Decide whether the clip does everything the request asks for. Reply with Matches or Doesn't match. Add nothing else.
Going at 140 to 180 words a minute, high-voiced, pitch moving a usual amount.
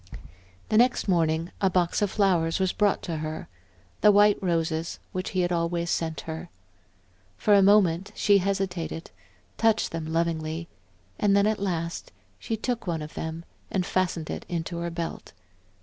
Doesn't match